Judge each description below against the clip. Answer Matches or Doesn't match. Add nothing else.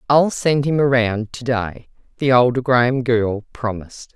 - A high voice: Doesn't match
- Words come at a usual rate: Matches